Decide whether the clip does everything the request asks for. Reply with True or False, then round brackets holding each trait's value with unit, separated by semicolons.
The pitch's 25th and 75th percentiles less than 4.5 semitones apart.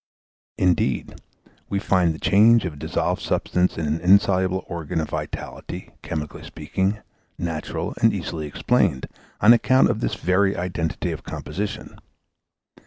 True (3.6 semitones)